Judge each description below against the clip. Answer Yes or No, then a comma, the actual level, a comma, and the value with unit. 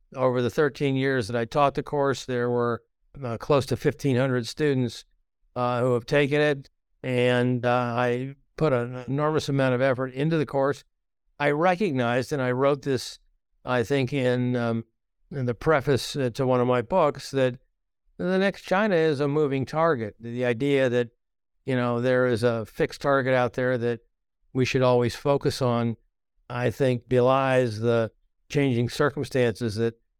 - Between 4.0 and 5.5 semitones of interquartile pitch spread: No, narrow, 2.6 semitones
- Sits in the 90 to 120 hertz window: No, low, 130 Hz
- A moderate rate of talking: Yes, average, 165 wpm